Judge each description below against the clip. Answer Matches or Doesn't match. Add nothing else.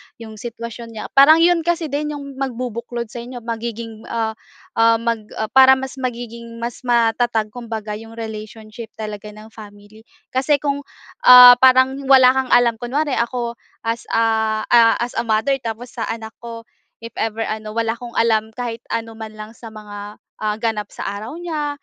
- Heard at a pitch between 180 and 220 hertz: Doesn't match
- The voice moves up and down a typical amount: Doesn't match